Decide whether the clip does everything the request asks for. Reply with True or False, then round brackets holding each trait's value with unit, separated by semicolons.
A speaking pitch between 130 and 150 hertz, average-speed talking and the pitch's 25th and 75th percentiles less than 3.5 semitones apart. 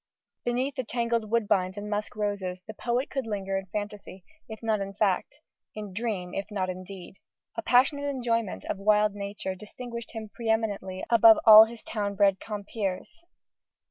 False (210 Hz; 170 wpm; 2.8 semitones)